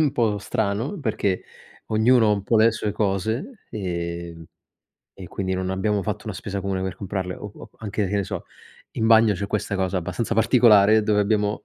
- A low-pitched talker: Yes, low, 105 Hz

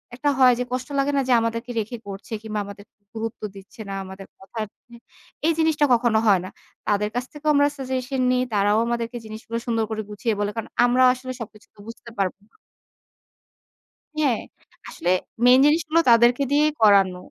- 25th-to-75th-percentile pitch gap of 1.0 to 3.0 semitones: No, average, 3.4 semitones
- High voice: Yes, high, 230 Hz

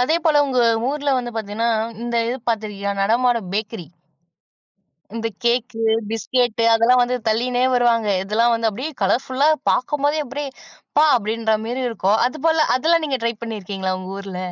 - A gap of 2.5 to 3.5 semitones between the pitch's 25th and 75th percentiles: Yes, average, 2.9 semitones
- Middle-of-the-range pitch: No, high, 235 Hz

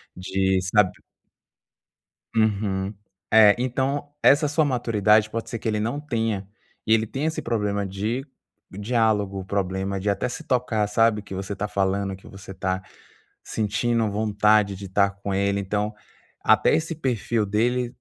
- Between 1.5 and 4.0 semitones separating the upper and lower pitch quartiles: Yes, average, 2.8 semitones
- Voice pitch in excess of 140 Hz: No, low, 105 Hz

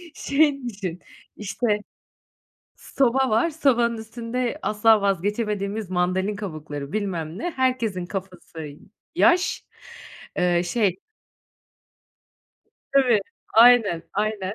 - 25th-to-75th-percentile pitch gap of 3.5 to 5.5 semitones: Yes, average, 4.7 semitones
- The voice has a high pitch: Yes, high, 210 Hz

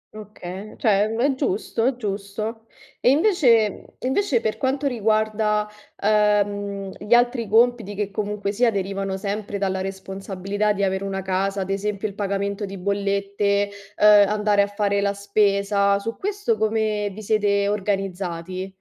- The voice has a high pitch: Yes, high, 205 Hz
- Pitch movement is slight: Yes, narrow, 1.6 semitones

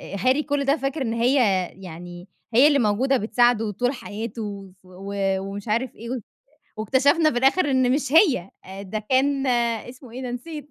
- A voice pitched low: No, high, 245 Hz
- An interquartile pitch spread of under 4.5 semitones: No, average, 5.1 semitones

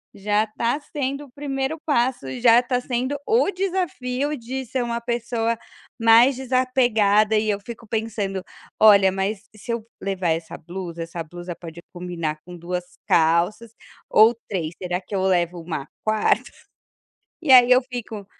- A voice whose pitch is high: Yes, high, 220 Hz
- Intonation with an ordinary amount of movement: No, wide, 5.7 semitones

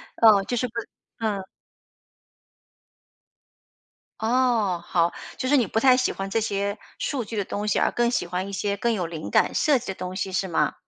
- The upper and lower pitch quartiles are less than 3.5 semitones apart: No, average, 3.8 semitones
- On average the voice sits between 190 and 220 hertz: Yes, high, 205 Hz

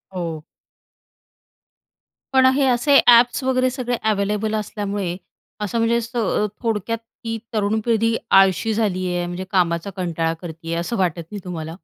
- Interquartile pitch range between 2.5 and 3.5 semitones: No, average, 4.7 semitones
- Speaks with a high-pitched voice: Yes, high, 210 Hz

